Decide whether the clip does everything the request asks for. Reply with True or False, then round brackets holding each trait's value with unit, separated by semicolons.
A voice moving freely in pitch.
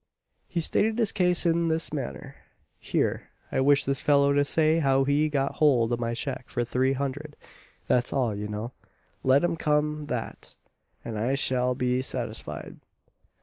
False (3.3 semitones)